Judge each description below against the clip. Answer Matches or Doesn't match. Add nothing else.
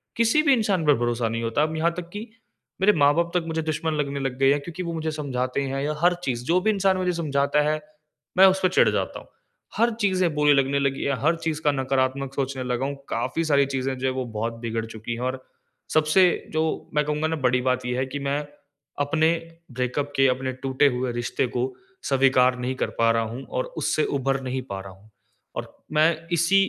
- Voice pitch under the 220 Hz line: Matches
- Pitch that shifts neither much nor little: Matches